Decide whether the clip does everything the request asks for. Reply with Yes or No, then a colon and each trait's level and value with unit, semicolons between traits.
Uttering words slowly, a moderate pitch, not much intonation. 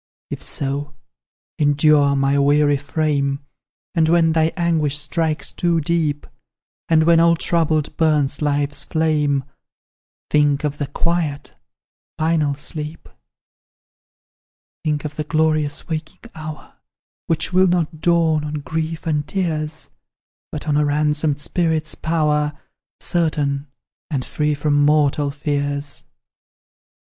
Yes: slow, 115 wpm; medium, 150 Hz; narrow, 1.9 semitones